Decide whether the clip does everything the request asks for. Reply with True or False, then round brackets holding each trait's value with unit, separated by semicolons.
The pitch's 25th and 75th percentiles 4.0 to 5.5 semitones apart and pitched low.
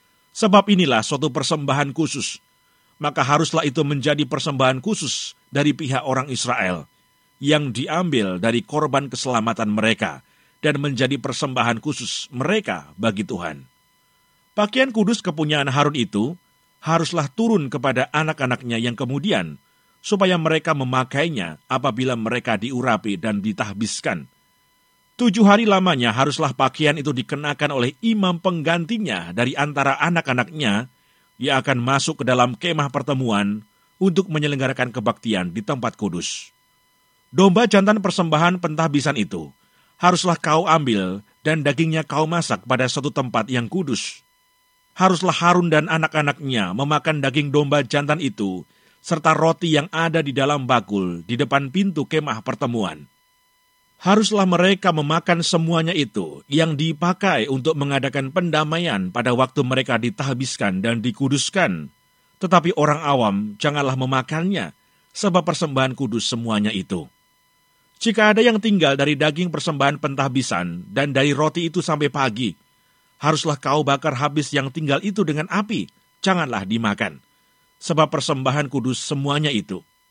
False (4.5 semitones; 145 Hz)